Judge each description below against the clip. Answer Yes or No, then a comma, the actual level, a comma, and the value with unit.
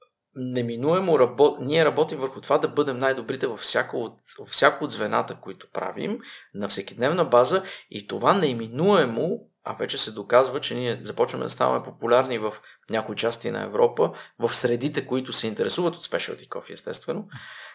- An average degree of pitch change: No, wide, 7.3 semitones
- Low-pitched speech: No, medium, 145 Hz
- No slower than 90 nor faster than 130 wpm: No, average, 160 wpm